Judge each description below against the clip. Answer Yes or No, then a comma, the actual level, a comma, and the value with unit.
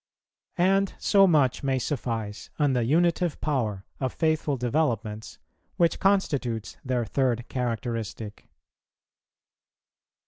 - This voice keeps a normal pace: No, slow, 100 wpm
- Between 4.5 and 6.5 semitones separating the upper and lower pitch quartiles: Yes, wide, 5.5 semitones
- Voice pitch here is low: Yes, low, 130 Hz